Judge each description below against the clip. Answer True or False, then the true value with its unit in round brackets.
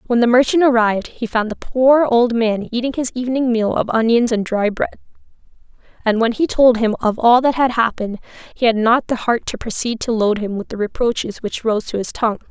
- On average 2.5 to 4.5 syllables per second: False (5.5 syllables/s)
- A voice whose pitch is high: True (235 Hz)